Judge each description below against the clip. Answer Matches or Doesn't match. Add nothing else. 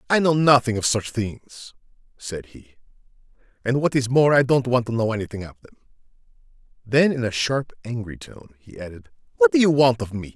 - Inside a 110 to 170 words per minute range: Doesn't match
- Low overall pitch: Matches